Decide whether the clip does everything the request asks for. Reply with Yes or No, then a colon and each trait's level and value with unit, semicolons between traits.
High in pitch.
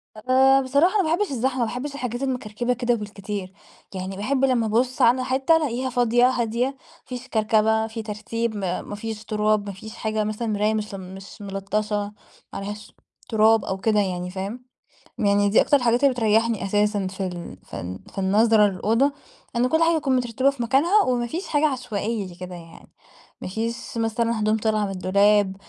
Yes: high, 220 Hz